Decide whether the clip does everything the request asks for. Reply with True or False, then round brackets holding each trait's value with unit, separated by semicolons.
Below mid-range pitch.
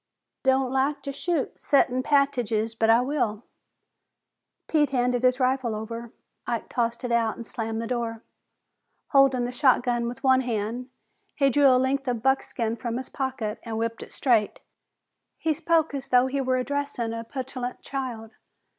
False (250 Hz)